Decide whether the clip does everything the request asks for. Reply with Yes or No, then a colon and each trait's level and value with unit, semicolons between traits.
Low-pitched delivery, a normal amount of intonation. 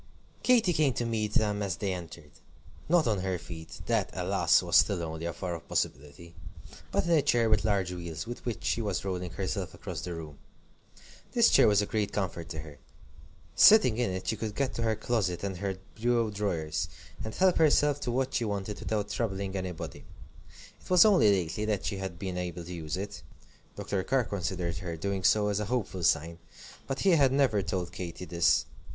Yes: low, 100 Hz; average, 4.5 semitones